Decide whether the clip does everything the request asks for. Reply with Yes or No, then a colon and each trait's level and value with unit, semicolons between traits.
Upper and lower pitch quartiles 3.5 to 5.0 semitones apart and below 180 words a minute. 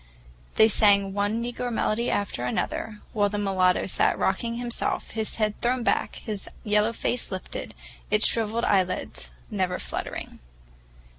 No: narrow, 2.6 semitones; average, 140 wpm